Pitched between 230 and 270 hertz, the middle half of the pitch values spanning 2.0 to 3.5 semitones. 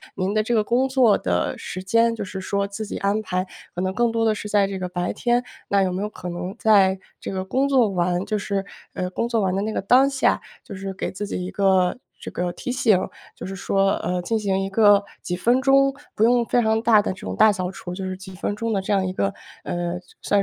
No: high, 200 Hz; average, 3.2 semitones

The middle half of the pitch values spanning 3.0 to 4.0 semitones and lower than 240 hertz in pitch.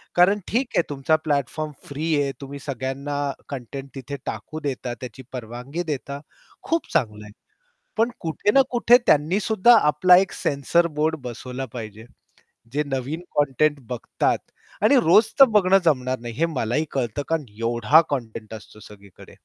No: average, 4.6 semitones; medium, 140 Hz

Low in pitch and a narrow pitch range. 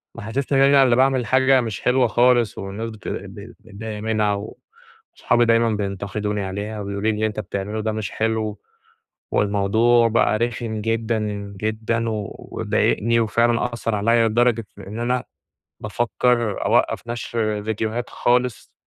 Yes: low, 110 Hz; narrow, 2.1 semitones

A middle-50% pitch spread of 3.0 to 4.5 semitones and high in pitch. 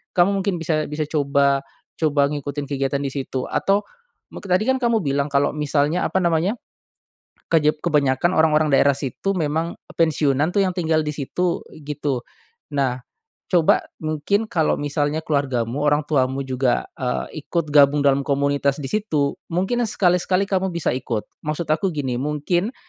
No: average, 3.5 semitones; medium, 150 Hz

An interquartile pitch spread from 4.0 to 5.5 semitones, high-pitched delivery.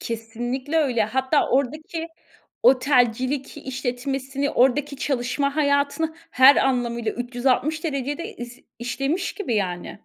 No: average, 2.8 semitones; very high, 265 Hz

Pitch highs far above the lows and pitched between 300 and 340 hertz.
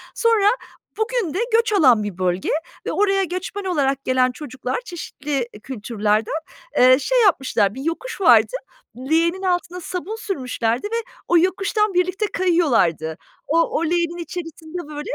Yes: wide, 6.8 semitones; very high, 335 Hz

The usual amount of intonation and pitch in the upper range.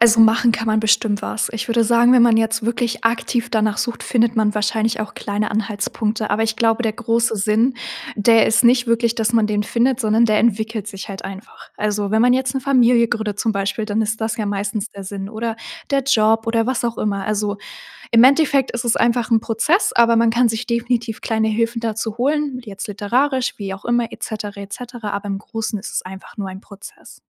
No: narrow, 1.9 semitones; high, 225 Hz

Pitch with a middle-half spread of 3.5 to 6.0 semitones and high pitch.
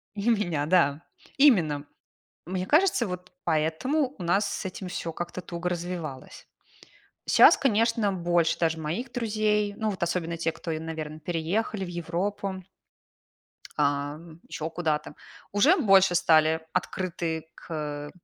No: average, 4.2 semitones; medium, 175 Hz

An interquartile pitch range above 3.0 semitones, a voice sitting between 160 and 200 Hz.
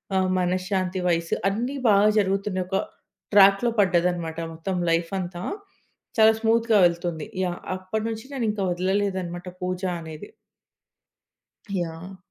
No: average, 2.7 semitones; medium, 185 Hz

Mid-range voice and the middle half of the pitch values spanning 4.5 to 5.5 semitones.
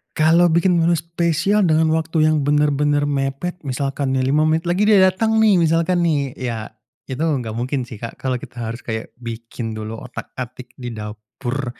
Yes: medium, 145 Hz; average, 5.2 semitones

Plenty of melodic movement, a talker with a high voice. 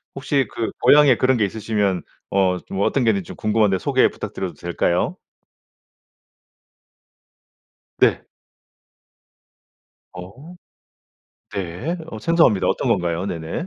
No: wide, 5.9 semitones; low, 100 Hz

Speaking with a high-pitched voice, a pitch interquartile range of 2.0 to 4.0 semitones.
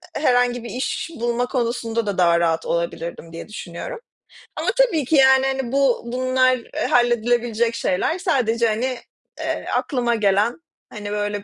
Yes: high, 235 Hz; average, 3.6 semitones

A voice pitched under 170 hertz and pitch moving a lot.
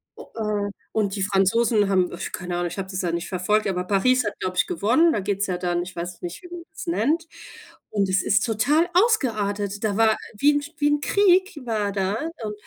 No: high, 210 Hz; wide, 7.0 semitones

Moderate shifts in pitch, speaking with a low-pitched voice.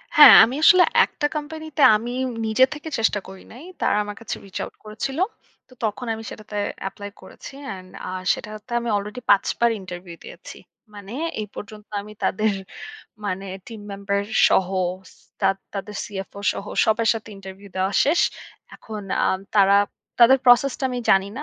No: average, 3.5 semitones; high, 215 Hz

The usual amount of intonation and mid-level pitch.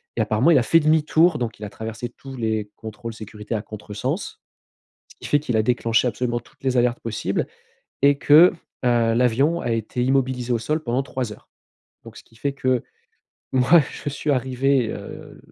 No: average, 3.3 semitones; low, 125 Hz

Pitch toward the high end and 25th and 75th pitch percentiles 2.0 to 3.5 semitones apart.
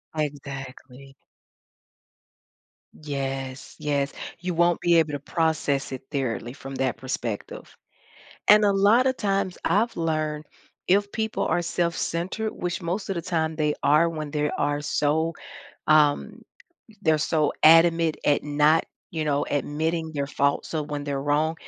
No: medium, 155 Hz; average, 2.9 semitones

